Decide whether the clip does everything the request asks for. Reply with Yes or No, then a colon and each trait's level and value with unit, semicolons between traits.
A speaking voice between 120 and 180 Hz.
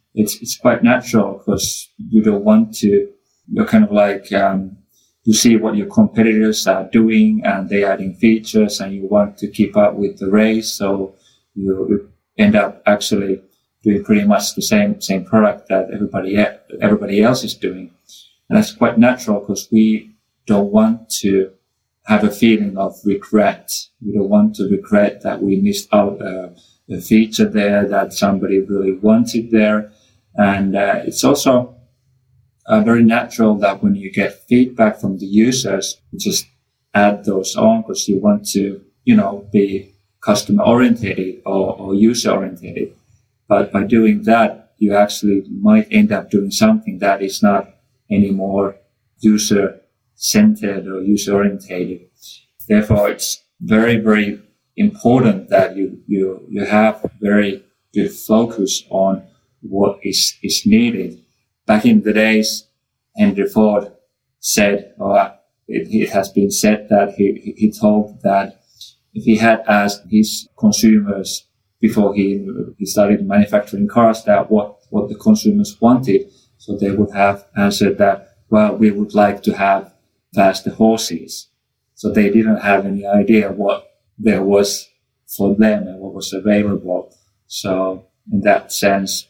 No: low, 105 Hz